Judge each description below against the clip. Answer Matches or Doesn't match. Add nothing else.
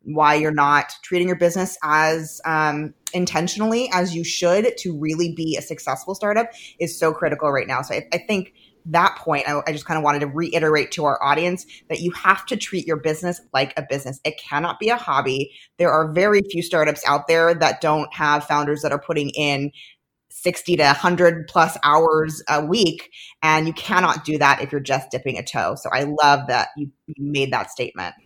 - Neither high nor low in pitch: Matches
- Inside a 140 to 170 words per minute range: Doesn't match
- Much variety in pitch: Doesn't match